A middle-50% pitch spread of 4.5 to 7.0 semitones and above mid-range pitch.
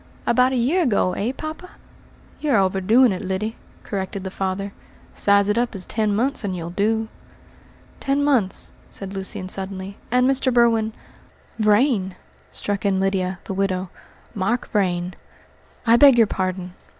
No: average, 4.0 semitones; high, 200 Hz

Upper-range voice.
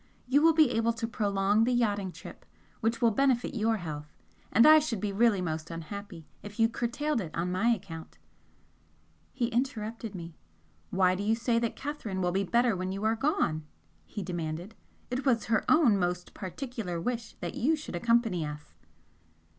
Yes: high, 220 Hz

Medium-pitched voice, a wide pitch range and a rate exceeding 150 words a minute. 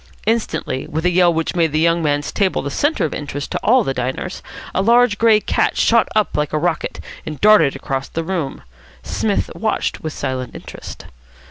Yes: medium, 165 Hz; wide, 6.2 semitones; average, 195 wpm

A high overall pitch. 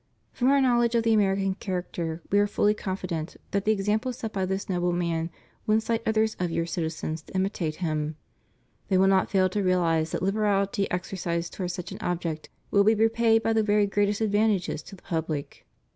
Yes: high, 195 Hz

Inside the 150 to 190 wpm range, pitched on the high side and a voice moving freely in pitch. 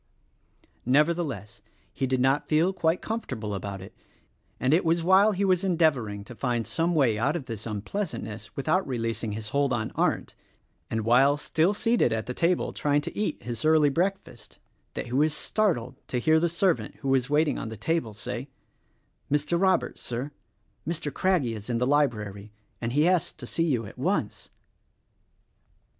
No: average, 180 wpm; medium, 140 Hz; wide, 6.3 semitones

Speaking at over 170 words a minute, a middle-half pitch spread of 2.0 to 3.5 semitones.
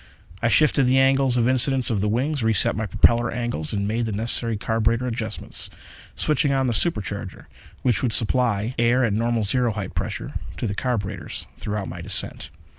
Yes: average, 185 wpm; average, 3.1 semitones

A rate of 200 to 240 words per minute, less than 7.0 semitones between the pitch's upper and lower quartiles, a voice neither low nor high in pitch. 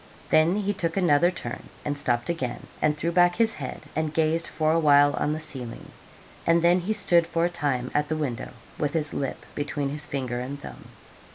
Yes: fast, 205 wpm; average, 3.0 semitones; medium, 155 Hz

